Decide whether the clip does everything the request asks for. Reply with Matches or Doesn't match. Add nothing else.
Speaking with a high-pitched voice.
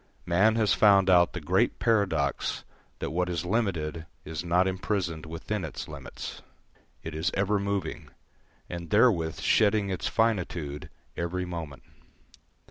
Doesn't match